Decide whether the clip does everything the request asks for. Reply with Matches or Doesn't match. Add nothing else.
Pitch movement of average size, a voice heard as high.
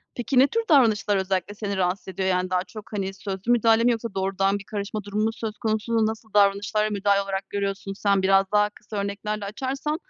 Doesn't match